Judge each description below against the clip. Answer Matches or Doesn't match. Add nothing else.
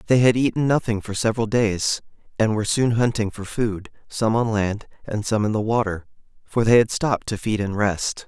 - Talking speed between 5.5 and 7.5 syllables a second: Doesn't match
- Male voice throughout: Matches